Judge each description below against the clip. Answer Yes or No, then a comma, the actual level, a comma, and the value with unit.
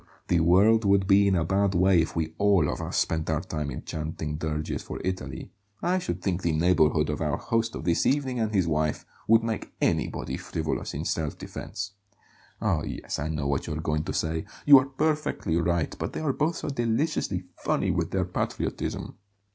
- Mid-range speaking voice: No, very low, 90 Hz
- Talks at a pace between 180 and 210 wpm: Yes, fast, 205 wpm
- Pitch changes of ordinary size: No, wide, 6.0 semitones